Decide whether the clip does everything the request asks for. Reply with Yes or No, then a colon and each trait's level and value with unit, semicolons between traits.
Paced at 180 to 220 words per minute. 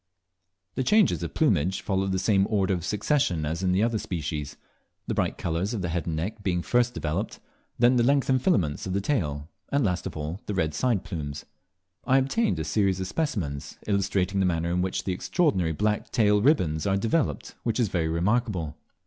Yes: average, 200 wpm